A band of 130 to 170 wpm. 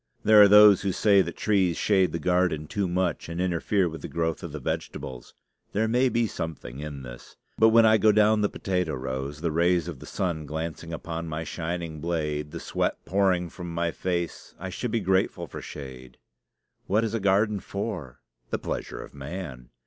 No: average, 195 wpm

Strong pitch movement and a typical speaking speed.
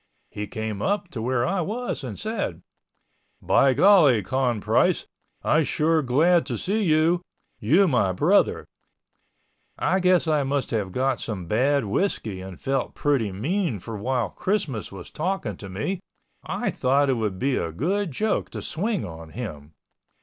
Yes: wide, 8.6 semitones; average, 160 wpm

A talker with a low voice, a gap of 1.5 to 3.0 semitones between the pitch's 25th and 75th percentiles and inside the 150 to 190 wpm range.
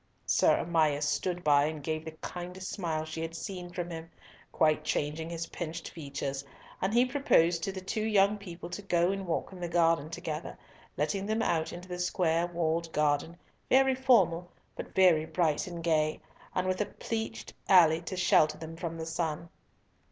No: medium, 170 Hz; narrow, 2.6 semitones; average, 180 wpm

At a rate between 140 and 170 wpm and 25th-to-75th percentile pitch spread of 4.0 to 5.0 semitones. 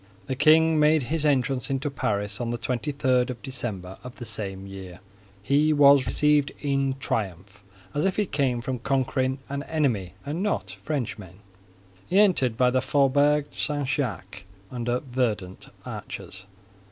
Yes: average, 155 wpm; average, 4.5 semitones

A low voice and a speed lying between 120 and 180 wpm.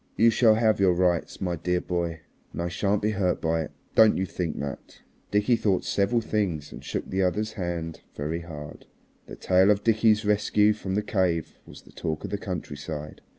No: very low, 95 Hz; average, 195 wpm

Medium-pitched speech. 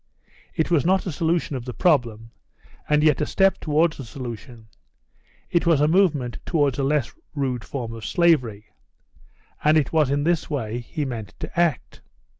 Yes: medium, 145 Hz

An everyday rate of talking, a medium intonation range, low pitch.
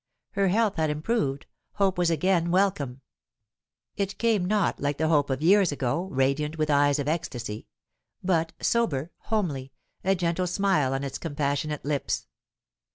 No: average, 150 wpm; average, 5.0 semitones; medium, 160 Hz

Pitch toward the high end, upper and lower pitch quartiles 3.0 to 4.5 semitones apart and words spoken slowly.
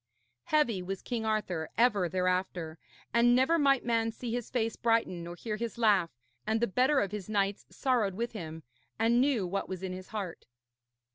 No: high, 215 Hz; average, 4.2 semitones; average, 185 wpm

